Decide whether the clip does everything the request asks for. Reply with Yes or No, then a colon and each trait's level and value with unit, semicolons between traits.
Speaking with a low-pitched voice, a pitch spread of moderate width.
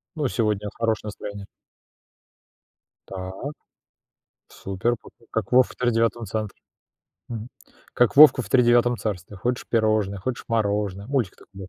Yes: low, 110 Hz; average, 3.1 semitones